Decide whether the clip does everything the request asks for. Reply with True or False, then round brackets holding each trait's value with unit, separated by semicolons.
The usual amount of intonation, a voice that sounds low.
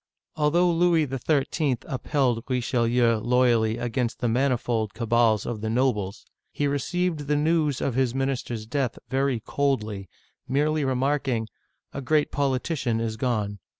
True (3.6 semitones; 130 Hz)